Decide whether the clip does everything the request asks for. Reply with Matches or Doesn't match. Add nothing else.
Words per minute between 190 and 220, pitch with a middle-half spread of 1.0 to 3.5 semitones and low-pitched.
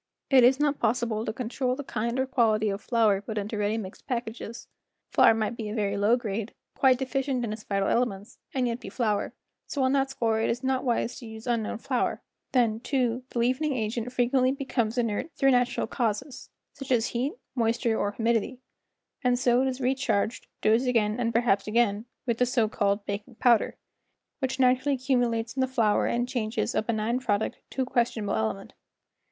Doesn't match